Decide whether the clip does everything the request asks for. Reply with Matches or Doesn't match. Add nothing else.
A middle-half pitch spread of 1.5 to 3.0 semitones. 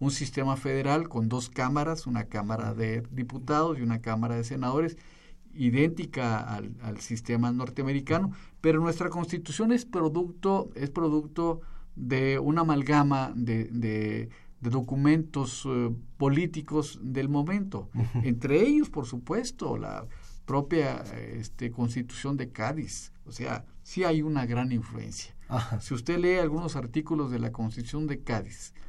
Doesn't match